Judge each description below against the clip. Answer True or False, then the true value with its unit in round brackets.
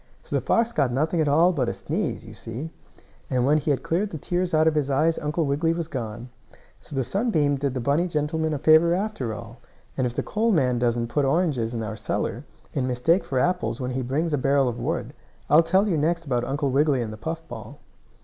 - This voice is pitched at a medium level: True (145 Hz)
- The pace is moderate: False (235 wpm)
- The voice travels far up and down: False (4.7 semitones)